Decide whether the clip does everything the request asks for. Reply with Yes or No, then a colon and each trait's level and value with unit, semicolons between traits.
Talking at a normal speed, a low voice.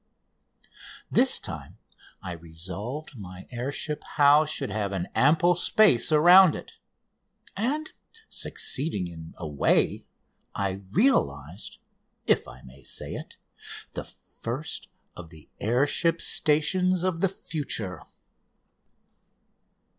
No: slow, 110 wpm; low, 130 Hz